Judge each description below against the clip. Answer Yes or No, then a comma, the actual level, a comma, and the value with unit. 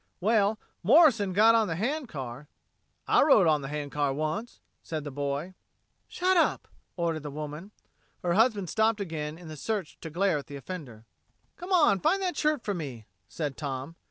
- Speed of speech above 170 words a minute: Yes, average, 185 wpm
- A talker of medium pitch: Yes, medium, 170 Hz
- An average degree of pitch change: No, wide, 6.9 semitones